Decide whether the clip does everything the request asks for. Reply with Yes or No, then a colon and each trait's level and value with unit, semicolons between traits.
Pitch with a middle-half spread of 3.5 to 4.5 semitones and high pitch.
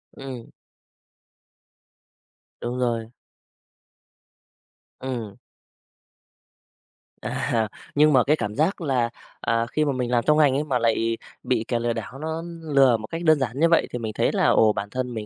No: average, 3.8 semitones; low, 125 Hz